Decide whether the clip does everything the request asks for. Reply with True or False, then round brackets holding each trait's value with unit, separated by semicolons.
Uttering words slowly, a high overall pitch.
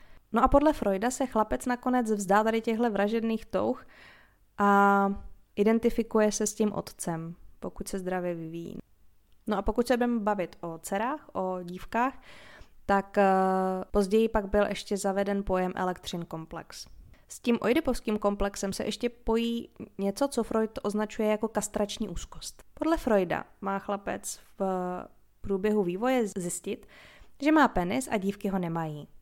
False (145 wpm; 205 Hz)